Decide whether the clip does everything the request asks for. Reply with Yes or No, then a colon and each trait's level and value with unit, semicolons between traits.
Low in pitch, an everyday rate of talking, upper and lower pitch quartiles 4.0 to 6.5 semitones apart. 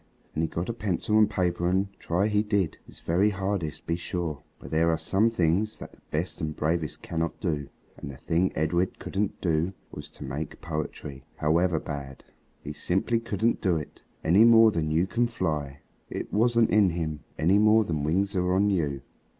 Yes: very low, 85 Hz; average, 190 wpm; average, 4.5 semitones